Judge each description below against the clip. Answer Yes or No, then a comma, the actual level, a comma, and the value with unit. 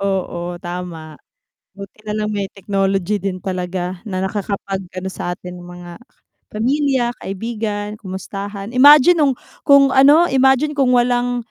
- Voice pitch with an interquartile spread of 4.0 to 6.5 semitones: Yes, average, 5.0 semitones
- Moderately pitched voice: No, high, 205 Hz